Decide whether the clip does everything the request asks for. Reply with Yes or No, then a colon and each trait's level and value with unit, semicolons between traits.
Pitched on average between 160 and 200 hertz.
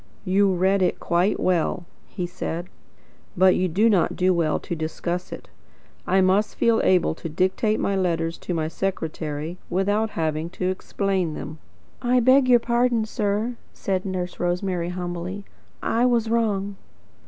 Yes: medium, 185 Hz